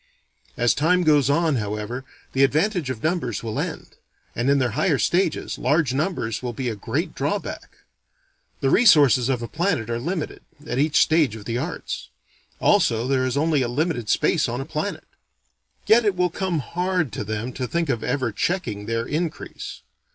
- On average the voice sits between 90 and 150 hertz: Yes, medium, 140 Hz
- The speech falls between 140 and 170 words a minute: No, average, 180 wpm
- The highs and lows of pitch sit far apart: Yes, wide, 5.8 semitones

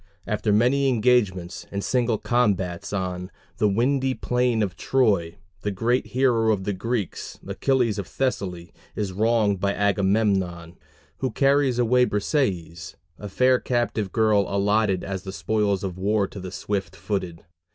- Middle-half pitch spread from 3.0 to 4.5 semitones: Yes, average, 4.1 semitones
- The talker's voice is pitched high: No, low, 105 Hz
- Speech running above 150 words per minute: No, average, 145 wpm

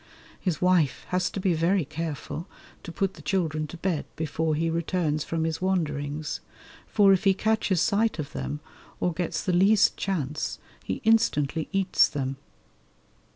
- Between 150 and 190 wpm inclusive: Yes, average, 155 wpm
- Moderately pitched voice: Yes, medium, 170 Hz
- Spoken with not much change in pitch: No, average, 3.8 semitones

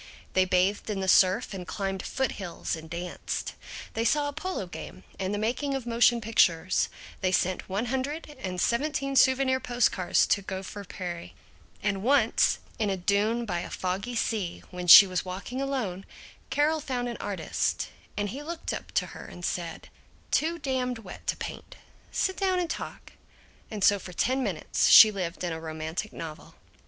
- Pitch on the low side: No, high, 205 Hz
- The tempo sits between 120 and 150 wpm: No, average, 175 wpm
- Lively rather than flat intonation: Yes, wide, 6.1 semitones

